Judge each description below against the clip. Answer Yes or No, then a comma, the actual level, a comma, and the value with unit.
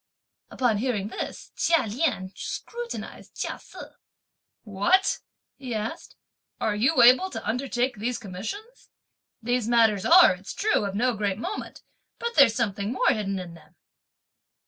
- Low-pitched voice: No, high, 235 Hz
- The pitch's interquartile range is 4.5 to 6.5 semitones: Yes, average, 4.9 semitones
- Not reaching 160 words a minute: Yes, average, 140 wpm